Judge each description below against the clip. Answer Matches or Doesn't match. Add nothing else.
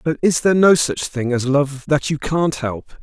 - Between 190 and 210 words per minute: Doesn't match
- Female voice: Doesn't match